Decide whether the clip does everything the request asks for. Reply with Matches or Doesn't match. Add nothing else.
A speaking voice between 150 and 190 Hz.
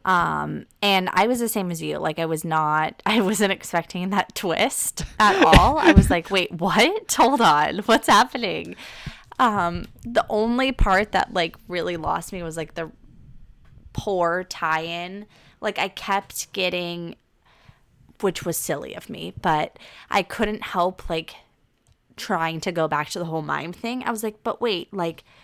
Matches